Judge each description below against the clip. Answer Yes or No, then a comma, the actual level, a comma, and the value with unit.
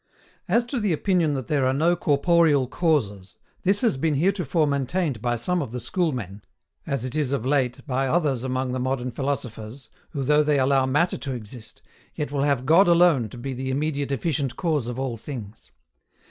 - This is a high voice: No, medium, 140 Hz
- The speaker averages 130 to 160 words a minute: No, average, 195 wpm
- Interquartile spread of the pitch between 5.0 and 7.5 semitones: No, average, 3.7 semitones